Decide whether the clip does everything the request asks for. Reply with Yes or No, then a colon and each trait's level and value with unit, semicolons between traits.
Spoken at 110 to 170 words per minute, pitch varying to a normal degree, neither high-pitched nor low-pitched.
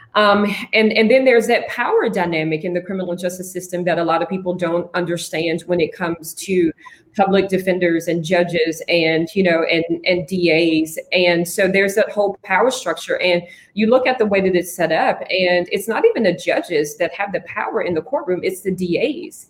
No: fast, 205 wpm; average, 3.0 semitones; medium, 180 Hz